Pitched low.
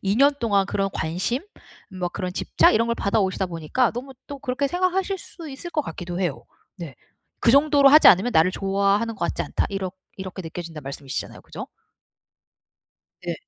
No: high, 200 Hz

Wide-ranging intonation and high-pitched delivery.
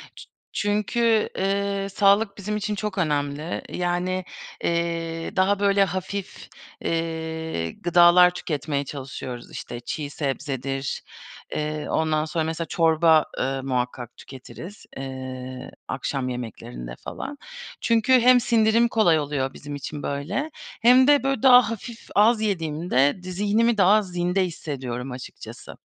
No: wide, 6.2 semitones; medium, 170 Hz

